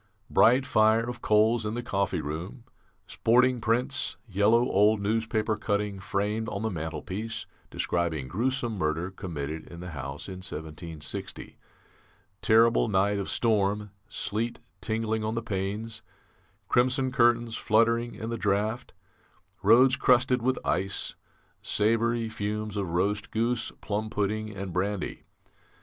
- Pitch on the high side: No, low, 105 Hz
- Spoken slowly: Yes, slow, 130 wpm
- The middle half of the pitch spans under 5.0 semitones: Yes, average, 3.0 semitones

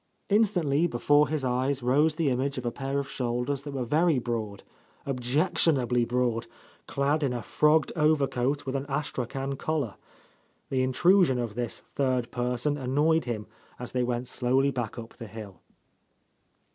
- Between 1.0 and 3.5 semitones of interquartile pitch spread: Yes, average, 3.1 semitones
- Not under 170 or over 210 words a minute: No, average, 160 wpm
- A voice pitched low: Yes, low, 130 Hz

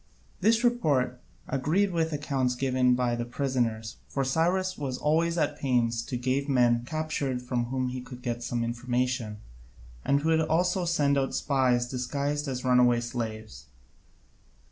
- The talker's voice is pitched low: Yes, low, 130 Hz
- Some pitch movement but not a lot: Yes, average, 3.4 semitones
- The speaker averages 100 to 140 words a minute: No, average, 155 wpm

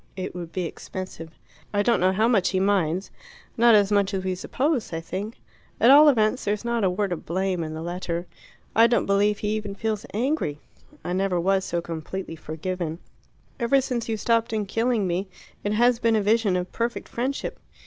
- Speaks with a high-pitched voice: Yes, high, 200 Hz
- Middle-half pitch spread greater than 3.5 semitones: Yes, average, 4.1 semitones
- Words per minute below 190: No, average, 200 wpm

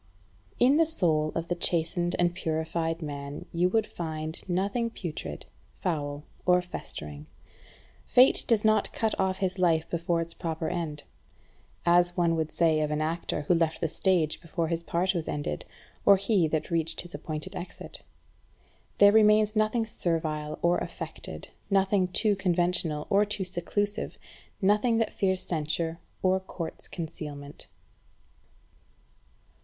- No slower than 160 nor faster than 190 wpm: No, average, 145 wpm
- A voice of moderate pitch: Yes, medium, 175 Hz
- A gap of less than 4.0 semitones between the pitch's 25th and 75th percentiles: Yes, average, 3.2 semitones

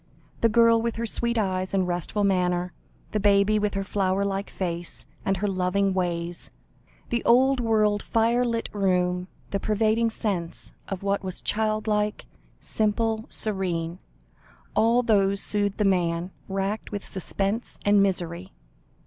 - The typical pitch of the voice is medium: No, high, 200 Hz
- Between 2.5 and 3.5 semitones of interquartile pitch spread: Yes, average, 2.8 semitones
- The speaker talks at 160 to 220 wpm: No, average, 140 wpm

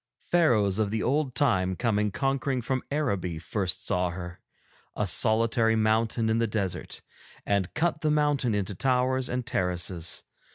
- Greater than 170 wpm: No, average, 150 wpm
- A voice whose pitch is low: Yes, low, 110 Hz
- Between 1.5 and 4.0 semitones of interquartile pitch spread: No, average, 5.2 semitones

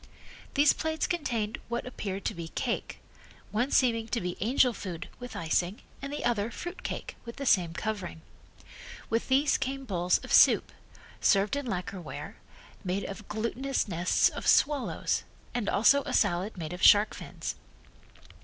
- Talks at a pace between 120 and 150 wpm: No, average, 160 wpm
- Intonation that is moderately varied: No, wide, 5.8 semitones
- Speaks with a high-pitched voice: Yes, high, 220 Hz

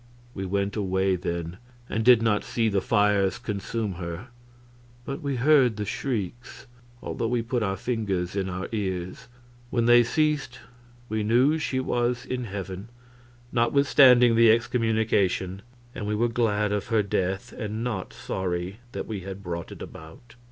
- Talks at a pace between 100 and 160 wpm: Yes, average, 155 wpm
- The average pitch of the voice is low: Yes, low, 110 Hz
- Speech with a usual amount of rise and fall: Yes, average, 3.9 semitones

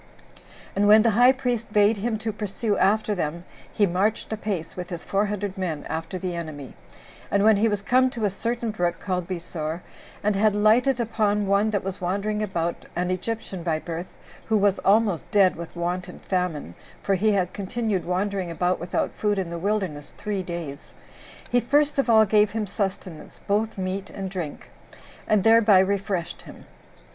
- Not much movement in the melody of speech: No, average, 3.2 semitones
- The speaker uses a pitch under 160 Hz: No, high, 200 Hz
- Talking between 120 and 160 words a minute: No, average, 180 wpm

